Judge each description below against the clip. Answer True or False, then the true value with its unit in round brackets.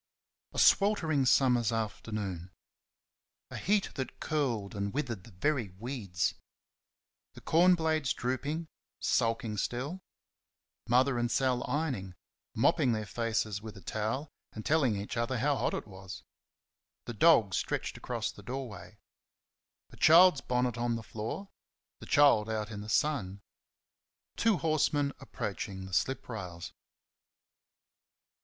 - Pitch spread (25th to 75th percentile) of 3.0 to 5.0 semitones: False (5.5 semitones)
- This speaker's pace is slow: True (130 wpm)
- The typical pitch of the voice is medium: False (120 Hz)